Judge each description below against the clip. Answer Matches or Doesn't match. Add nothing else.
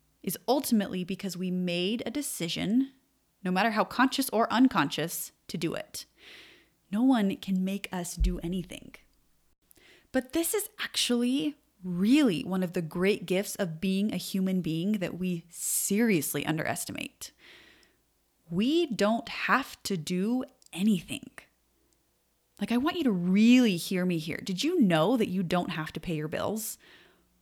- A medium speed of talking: Matches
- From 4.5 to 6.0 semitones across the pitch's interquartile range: Matches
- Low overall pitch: Doesn't match